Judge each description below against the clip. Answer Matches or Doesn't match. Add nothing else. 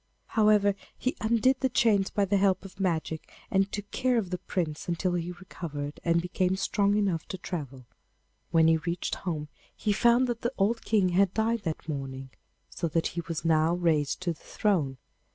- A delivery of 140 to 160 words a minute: Doesn't match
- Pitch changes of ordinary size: Matches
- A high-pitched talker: Doesn't match